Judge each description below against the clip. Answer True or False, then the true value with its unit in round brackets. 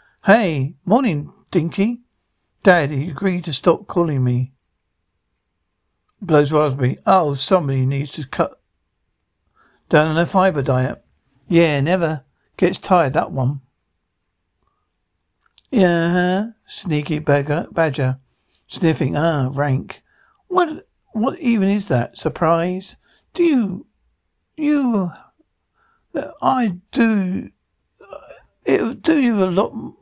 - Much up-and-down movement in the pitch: True (6.6 semitones)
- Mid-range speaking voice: True (165 Hz)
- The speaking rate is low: True (100 wpm)